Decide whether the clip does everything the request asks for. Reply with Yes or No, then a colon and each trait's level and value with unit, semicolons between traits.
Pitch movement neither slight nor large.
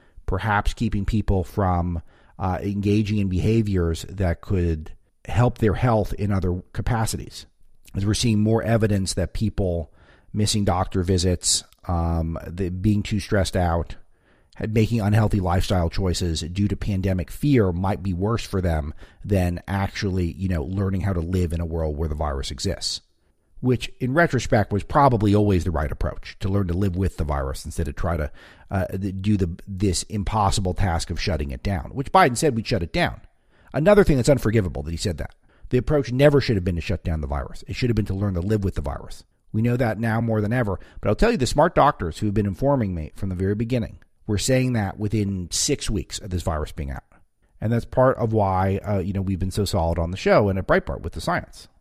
Yes: average, 3.7 semitones